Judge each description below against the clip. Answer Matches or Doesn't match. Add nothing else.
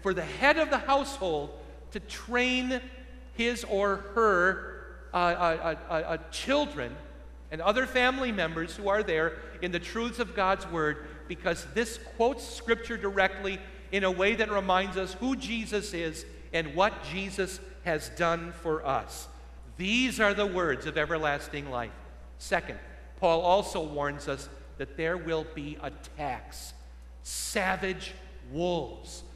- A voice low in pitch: Doesn't match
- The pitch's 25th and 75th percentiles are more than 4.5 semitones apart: Matches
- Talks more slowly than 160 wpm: Matches